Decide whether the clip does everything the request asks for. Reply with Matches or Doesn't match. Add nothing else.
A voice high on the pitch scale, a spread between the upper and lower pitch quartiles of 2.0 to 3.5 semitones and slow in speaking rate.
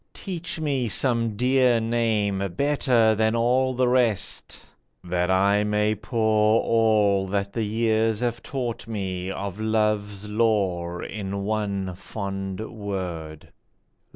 Doesn't match